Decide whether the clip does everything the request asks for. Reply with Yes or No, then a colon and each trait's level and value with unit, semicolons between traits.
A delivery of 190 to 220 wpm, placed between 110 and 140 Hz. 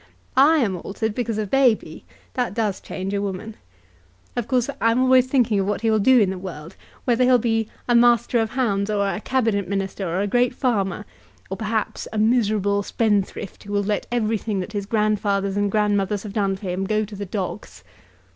No: average, 200 wpm; high, 210 Hz